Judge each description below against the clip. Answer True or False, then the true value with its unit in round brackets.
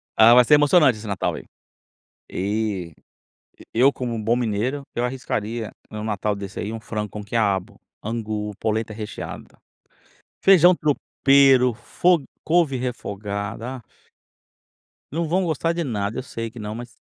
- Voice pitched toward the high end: False (115 Hz)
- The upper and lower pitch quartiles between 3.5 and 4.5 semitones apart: True (4.0 semitones)